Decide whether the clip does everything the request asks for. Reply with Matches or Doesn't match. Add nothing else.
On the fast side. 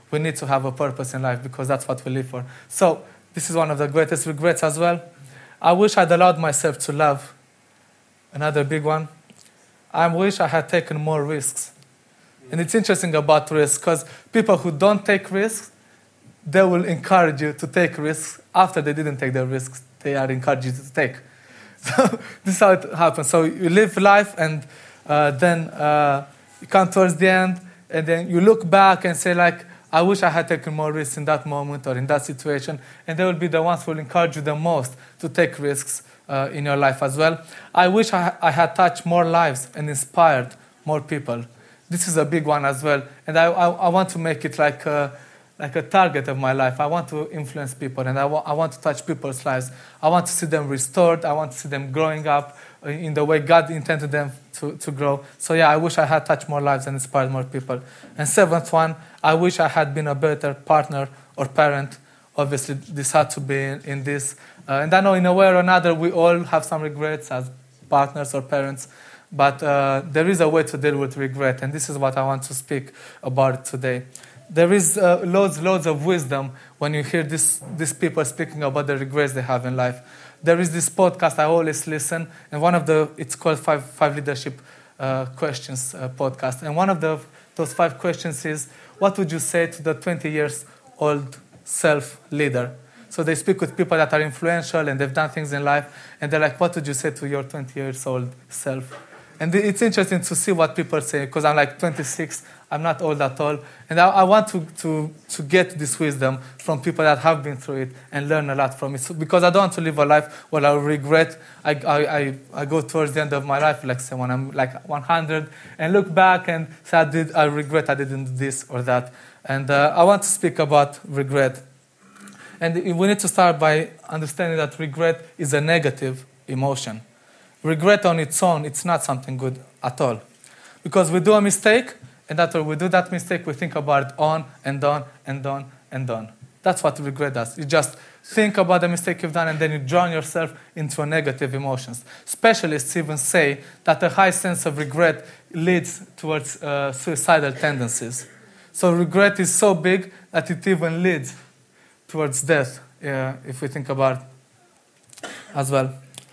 Matches